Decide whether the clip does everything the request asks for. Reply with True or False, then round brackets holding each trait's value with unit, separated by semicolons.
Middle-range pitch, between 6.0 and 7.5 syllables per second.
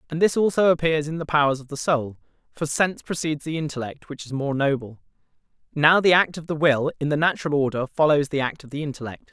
True (150 Hz; 6.3 syllables/s)